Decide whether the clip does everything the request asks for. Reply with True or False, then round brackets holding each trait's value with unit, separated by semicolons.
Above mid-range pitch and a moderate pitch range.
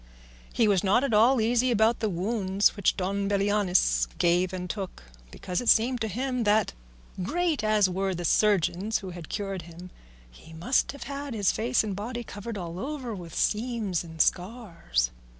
True (205 Hz; 4.3 semitones)